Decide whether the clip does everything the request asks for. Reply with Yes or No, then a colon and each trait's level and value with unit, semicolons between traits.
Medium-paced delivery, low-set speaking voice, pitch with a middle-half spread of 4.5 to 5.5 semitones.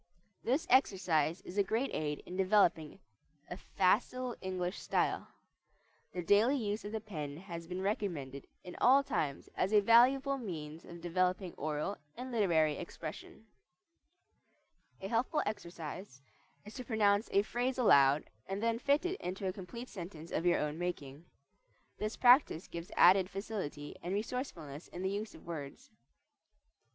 No: average, 150 wpm; high, 190 Hz; average, 5.2 semitones